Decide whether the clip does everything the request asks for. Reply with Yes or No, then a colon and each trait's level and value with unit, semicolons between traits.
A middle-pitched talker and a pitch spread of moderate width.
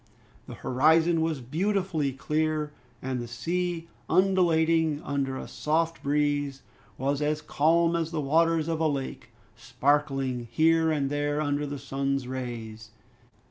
Yes: medium, 150 Hz; average, 3.1 semitones